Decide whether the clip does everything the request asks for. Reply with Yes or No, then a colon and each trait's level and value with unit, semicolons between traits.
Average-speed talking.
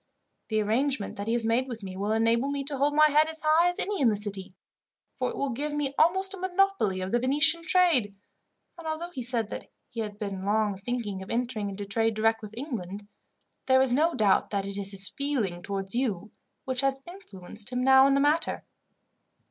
No: fast, 215 wpm